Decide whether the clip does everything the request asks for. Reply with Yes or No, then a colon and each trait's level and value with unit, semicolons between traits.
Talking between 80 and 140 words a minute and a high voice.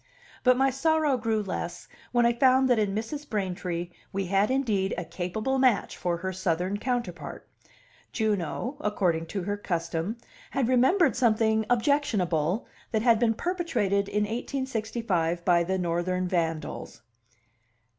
Yes: slow, 135 wpm; high, 210 Hz